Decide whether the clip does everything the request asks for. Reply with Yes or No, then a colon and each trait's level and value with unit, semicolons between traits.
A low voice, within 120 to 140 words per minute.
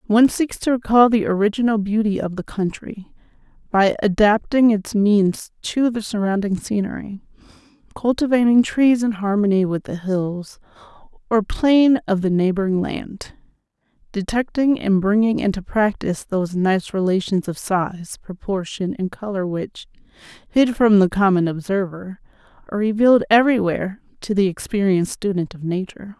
No: high, 205 Hz; slow, 135 wpm